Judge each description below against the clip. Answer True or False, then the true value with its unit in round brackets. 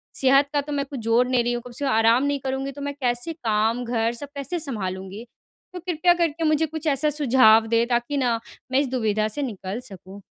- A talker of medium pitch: False (255 Hz)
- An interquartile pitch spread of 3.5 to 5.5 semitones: True (3.9 semitones)